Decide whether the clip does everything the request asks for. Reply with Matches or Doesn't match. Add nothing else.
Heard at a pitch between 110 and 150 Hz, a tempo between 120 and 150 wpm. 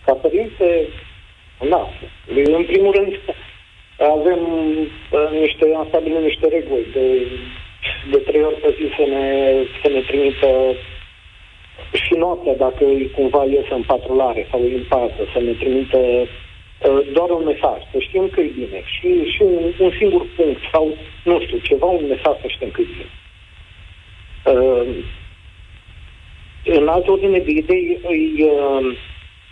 Matches